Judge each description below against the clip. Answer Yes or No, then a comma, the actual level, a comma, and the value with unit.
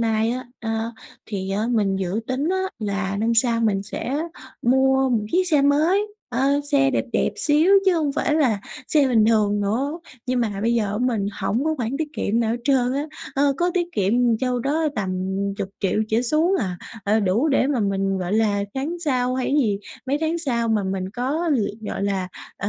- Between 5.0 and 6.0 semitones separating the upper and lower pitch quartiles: Yes, average, 5.3 semitones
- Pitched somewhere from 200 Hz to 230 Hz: No, high, 240 Hz